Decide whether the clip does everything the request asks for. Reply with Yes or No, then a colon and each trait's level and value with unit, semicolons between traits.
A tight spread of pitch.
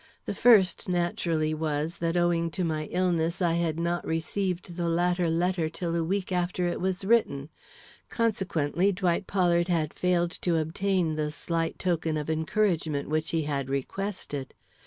Yes: narrow, 2.3 semitones